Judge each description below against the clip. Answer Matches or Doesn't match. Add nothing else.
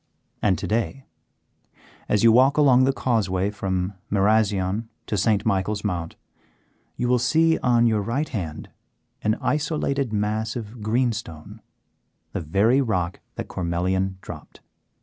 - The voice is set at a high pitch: Doesn't match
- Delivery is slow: Matches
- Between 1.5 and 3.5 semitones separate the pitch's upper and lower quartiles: Doesn't match